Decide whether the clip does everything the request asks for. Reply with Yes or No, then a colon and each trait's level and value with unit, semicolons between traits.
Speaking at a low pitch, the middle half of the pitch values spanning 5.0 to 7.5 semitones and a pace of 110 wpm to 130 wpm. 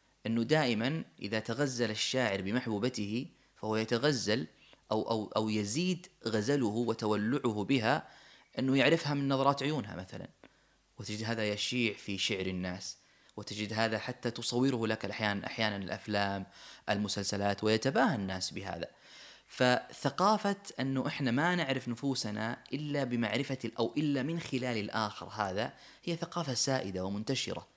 No: low, 115 Hz; average, 4.3 semitones; average, 125 wpm